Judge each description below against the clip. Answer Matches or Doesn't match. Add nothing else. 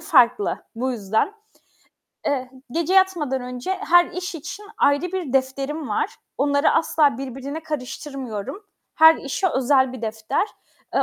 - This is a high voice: Matches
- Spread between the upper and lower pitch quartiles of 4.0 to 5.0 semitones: Matches